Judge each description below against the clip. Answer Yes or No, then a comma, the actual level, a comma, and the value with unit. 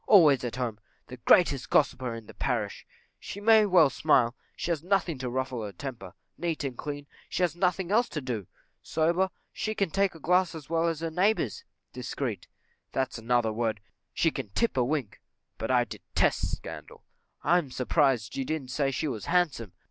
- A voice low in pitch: No, medium, 145 Hz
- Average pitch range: No, wide, 5.8 semitones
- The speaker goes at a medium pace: Yes, average, 185 wpm